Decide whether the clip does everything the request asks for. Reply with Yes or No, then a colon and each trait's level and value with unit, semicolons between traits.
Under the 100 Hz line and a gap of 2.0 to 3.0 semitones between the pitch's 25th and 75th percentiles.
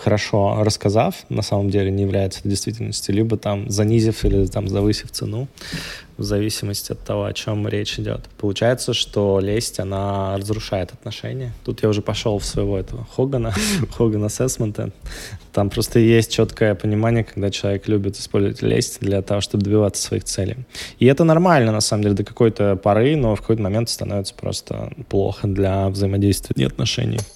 No: low, 105 Hz; narrow, 2.4 semitones